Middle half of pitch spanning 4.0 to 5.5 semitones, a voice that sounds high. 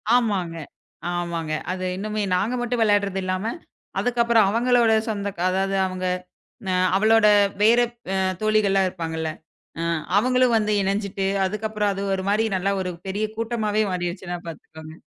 No: average, 3.1 semitones; high, 200 Hz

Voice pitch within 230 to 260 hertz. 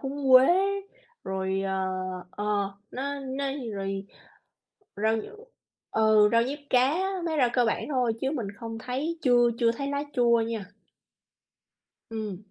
Yes: high, 235 Hz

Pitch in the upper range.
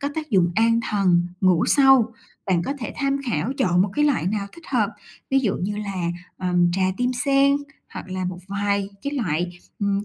Yes: high, 200 Hz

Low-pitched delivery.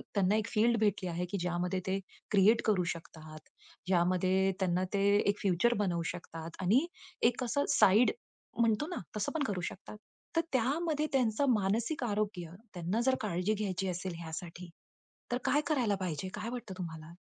No: high, 195 Hz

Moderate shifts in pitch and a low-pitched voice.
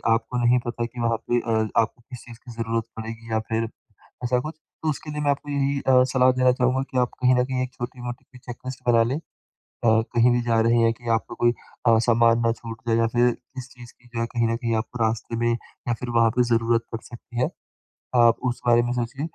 No: narrow, 1.5 semitones; low, 120 Hz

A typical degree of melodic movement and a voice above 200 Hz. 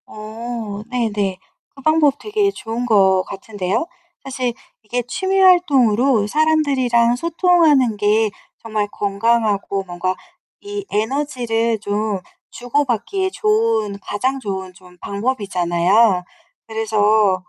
Yes: average, 5.0 semitones; high, 225 Hz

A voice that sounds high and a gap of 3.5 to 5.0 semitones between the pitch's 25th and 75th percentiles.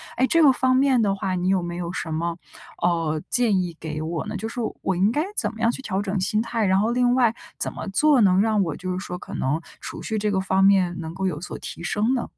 Yes: high, 195 Hz; average, 4.5 semitones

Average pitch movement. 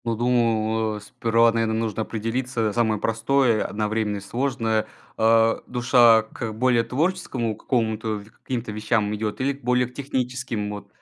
No: narrow, 2.3 semitones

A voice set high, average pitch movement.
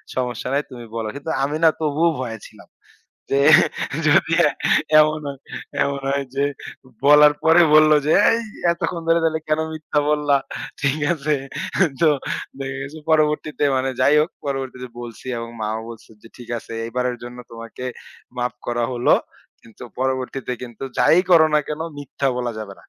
No: medium, 140 Hz; average, 3.7 semitones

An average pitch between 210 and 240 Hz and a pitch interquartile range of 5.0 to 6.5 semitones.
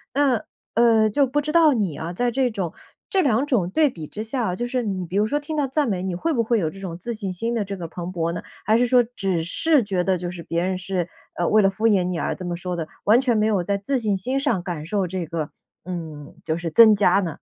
No: high, 200 Hz; average, 5.3 semitones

